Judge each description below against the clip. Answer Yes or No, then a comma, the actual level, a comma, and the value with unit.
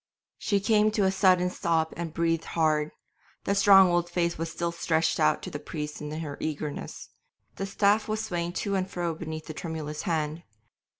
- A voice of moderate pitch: Yes, medium, 170 Hz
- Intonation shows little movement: No, average, 3.3 semitones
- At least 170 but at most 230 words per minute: Yes, average, 185 wpm